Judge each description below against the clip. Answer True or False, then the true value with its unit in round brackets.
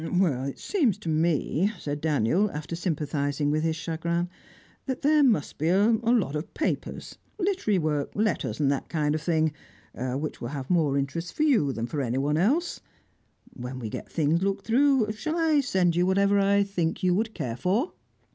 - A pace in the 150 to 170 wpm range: False (180 wpm)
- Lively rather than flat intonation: True (6.1 semitones)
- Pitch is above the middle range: False (170 Hz)